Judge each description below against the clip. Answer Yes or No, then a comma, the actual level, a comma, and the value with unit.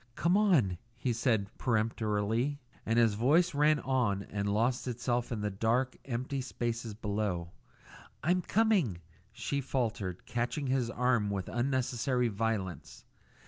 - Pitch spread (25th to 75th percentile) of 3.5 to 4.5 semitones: Yes, average, 4.0 semitones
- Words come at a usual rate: No, slow, 130 wpm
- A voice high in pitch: No, low, 120 Hz